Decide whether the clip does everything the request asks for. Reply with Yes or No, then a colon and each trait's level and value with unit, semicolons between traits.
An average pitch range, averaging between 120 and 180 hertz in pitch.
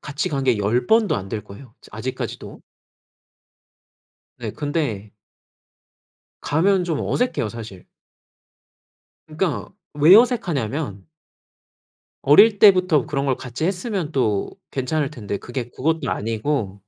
No: wide, 6.7 semitones; medium, 140 Hz